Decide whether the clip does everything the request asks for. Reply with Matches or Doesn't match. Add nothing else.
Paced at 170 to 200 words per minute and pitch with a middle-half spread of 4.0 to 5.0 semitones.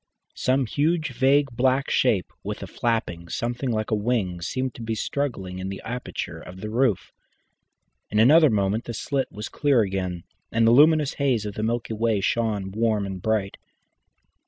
Matches